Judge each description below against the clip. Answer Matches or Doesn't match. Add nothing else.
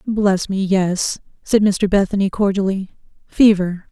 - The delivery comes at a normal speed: Doesn't match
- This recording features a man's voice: Doesn't match